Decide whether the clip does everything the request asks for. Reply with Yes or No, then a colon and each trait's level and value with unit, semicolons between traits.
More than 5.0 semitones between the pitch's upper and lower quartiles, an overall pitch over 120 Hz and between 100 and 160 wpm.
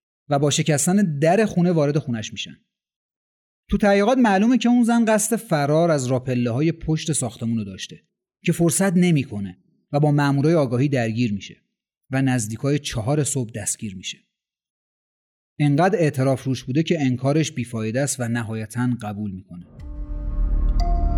Yes: wide, 5.6 semitones; medium, 140 Hz; average, 140 wpm